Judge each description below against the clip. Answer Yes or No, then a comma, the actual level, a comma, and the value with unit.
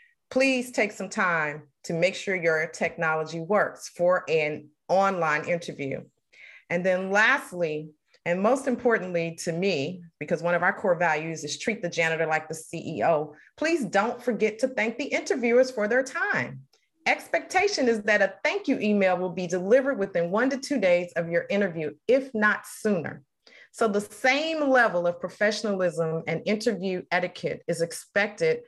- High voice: Yes, high, 195 Hz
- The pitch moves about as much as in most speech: No, wide, 6.2 semitones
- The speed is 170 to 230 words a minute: No, average, 160 wpm